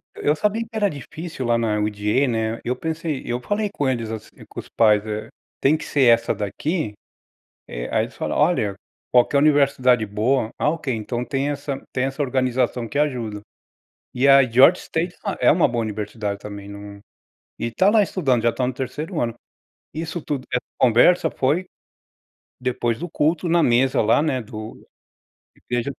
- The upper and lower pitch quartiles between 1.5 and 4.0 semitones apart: No, average, 4.9 semitones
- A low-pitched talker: Yes, low, 130 Hz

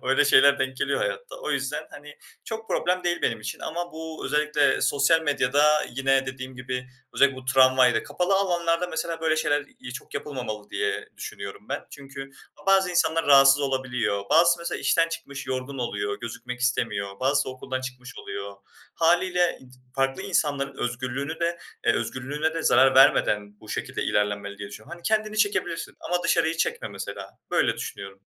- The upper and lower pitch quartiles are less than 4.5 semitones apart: No, average, 4.8 semitones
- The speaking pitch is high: No, medium, 140 Hz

